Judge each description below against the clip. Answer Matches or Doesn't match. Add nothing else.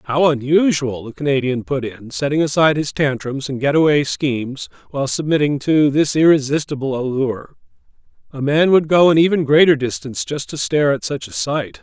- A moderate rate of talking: Matches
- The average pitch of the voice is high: Doesn't match